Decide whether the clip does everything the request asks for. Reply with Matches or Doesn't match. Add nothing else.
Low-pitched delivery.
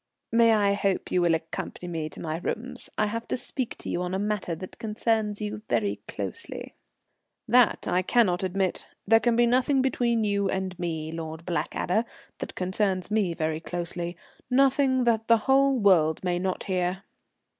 Doesn't match